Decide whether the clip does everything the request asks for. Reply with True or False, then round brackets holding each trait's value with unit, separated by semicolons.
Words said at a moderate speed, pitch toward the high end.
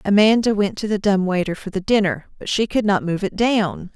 False (245 wpm; 200 Hz)